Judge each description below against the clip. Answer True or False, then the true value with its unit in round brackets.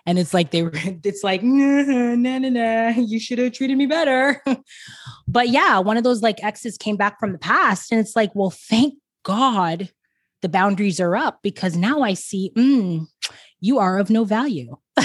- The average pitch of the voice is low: False (220 Hz)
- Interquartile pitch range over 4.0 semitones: True (5.0 semitones)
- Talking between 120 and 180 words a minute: False (190 wpm)